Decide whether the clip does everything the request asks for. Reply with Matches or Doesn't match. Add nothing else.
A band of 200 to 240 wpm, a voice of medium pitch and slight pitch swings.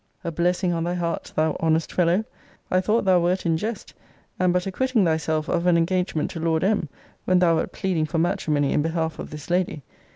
Matches